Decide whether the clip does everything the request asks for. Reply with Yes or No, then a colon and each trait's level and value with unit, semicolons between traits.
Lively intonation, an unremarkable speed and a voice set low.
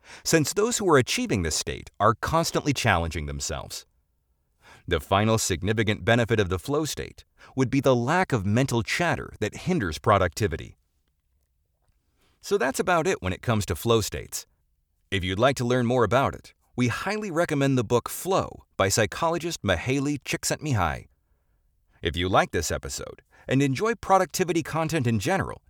Yes: wide, 8.6 semitones; average, 160 wpm; low, 115 Hz